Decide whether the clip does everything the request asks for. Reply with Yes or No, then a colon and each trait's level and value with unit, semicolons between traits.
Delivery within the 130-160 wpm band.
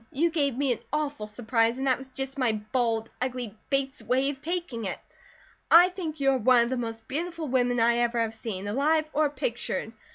No: fast, 205 wpm